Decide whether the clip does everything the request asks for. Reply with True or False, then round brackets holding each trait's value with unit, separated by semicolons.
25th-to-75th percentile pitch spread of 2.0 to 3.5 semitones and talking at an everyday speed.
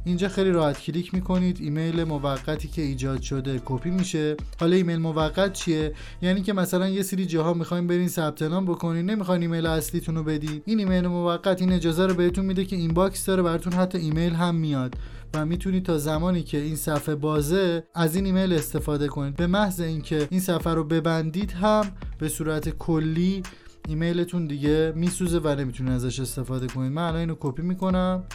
False (2.9 semitones; 180 wpm)